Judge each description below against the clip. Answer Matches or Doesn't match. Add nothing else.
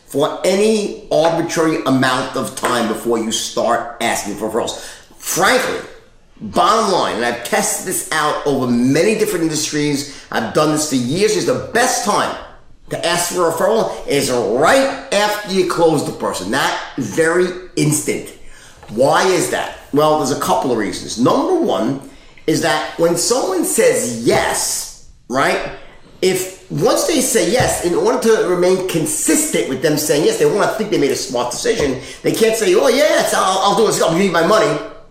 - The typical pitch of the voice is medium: Matches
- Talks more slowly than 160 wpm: Doesn't match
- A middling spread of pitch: Doesn't match